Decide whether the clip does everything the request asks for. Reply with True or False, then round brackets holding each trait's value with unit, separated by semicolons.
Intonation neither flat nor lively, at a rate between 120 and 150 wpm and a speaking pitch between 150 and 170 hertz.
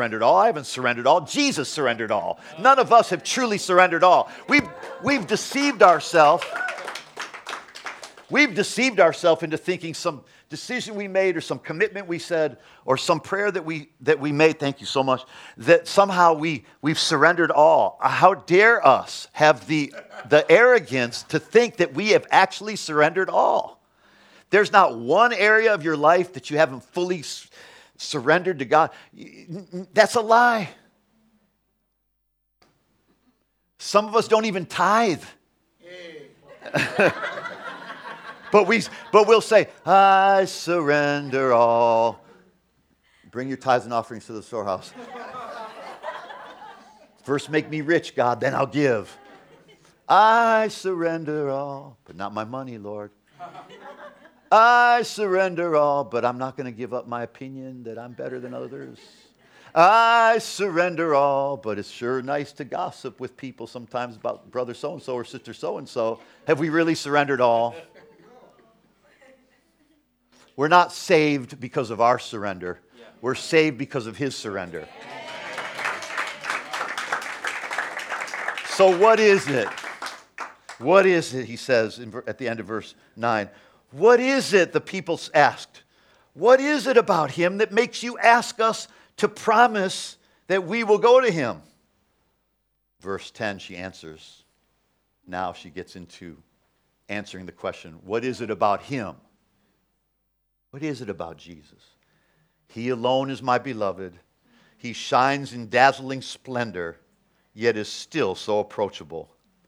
False (8.1 semitones; 140 wpm; 155 Hz)